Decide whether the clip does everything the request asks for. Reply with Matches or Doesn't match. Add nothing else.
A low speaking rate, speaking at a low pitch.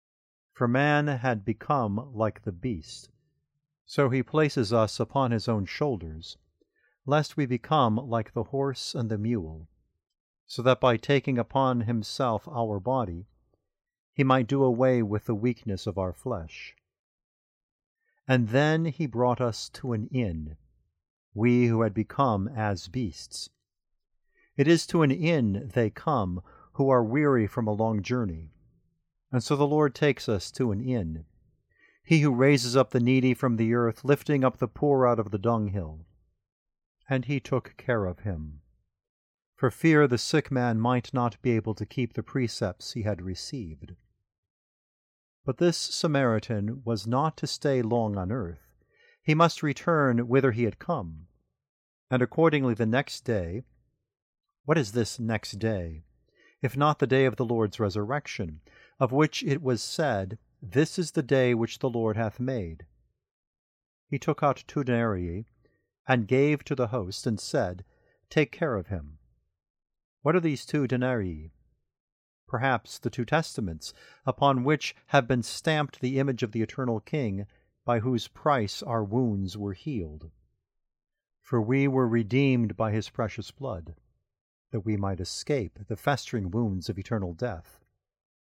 Doesn't match